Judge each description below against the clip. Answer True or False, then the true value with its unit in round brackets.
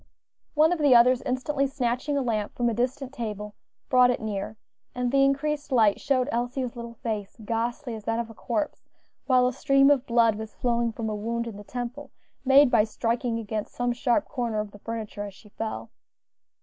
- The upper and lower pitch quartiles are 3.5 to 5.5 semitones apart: False (2.9 semitones)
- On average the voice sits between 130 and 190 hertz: False (240 Hz)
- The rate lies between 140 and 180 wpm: False (200 wpm)